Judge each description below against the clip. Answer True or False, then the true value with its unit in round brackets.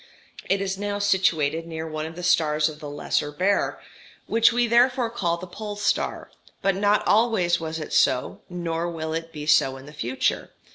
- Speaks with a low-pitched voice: False (170 Hz)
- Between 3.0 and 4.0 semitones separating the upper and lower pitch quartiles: False (4.6 semitones)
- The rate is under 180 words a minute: False (190 wpm)